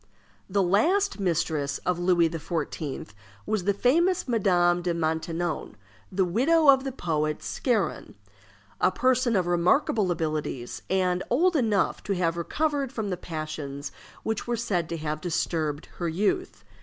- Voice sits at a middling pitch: Yes, medium, 180 Hz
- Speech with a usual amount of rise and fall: No, wide, 6.2 semitones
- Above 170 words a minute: No, average, 145 wpm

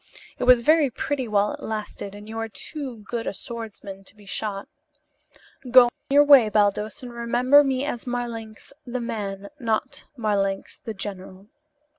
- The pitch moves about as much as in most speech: Yes, average, 3.4 semitones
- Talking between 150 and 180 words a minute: Yes, average, 160 wpm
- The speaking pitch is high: Yes, high, 225 Hz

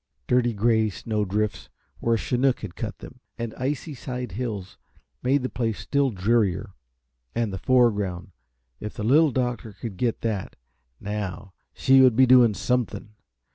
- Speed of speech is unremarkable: Yes, average, 155 wpm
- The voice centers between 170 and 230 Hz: No, low, 115 Hz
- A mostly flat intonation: No, average, 3.5 semitones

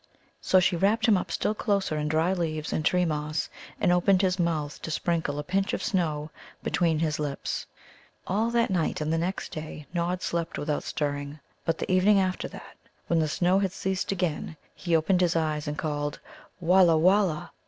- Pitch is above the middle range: No, medium, 170 Hz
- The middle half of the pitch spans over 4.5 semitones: No, average, 3.3 semitones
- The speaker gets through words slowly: No, average, 190 wpm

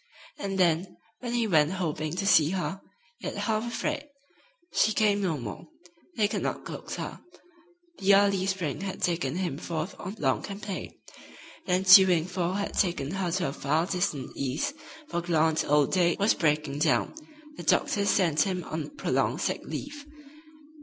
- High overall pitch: No, medium, 180 Hz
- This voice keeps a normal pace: Yes, average, 165 wpm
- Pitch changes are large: No, average, 3.9 semitones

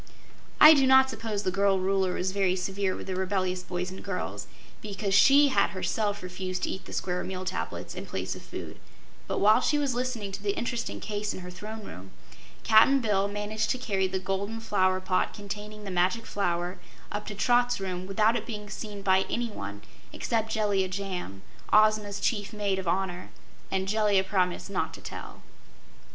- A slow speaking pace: No, average, 185 wpm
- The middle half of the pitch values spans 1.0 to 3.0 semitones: Yes, narrow, 2.5 semitones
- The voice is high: Yes, high, 200 Hz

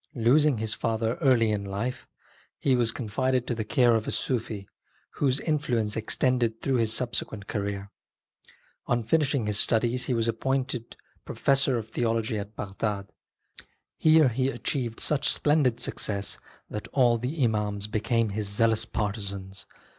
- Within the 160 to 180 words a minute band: No, average, 150 wpm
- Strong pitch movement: No, average, 3.2 semitones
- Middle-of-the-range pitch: No, low, 115 Hz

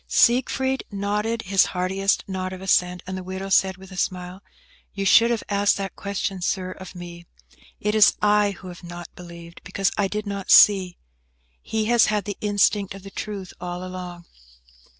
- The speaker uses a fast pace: No, average, 180 wpm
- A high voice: Yes, high, 195 Hz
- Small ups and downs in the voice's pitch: Yes, narrow, 2.0 semitones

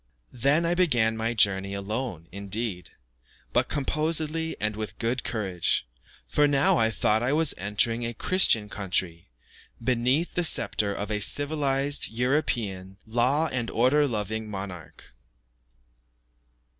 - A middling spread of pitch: No, wide, 5.7 semitones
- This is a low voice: Yes, low, 115 Hz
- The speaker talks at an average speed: No, slow, 125 wpm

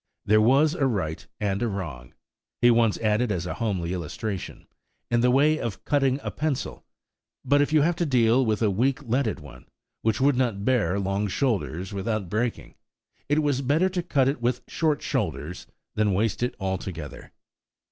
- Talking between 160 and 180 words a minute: Yes, average, 170 wpm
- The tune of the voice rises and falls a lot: Yes, wide, 5.7 semitones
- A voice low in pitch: Yes, low, 115 Hz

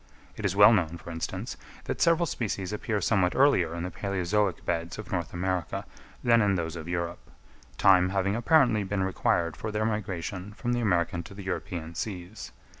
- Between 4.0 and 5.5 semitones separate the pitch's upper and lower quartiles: No, average, 3.5 semitones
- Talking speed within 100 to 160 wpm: No, average, 185 wpm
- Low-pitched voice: Yes, very low, 95 Hz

